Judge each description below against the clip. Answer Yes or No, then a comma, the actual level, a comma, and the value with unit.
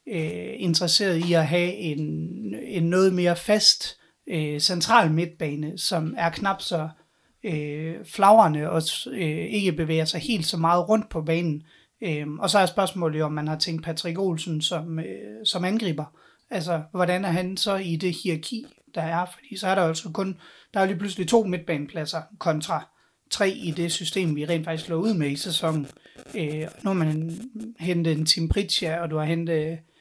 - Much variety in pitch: No, average, 3.0 semitones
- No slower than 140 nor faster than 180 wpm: No, average, 190 wpm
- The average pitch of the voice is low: No, medium, 170 Hz